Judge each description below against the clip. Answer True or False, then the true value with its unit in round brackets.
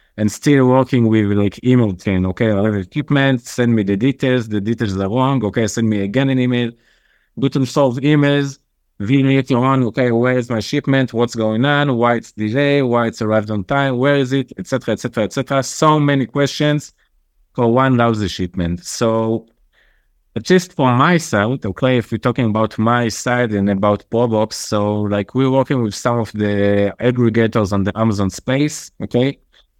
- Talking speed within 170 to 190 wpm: True (175 wpm)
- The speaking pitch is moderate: False (120 Hz)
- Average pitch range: True (4.0 semitones)